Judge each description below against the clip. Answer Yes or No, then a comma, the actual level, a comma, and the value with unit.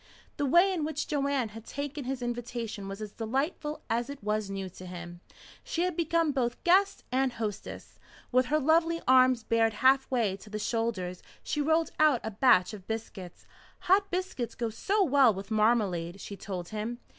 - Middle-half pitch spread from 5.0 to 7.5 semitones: Yes, wide, 5.6 semitones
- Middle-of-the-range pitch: No, high, 240 Hz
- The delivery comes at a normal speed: Yes, average, 180 wpm